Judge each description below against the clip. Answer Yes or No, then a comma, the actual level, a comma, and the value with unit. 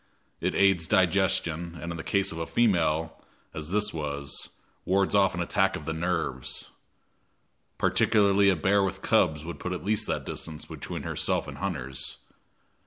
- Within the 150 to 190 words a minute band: Yes, average, 160 wpm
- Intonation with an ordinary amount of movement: Yes, average, 3.5 semitones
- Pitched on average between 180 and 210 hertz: No, very low, 85 Hz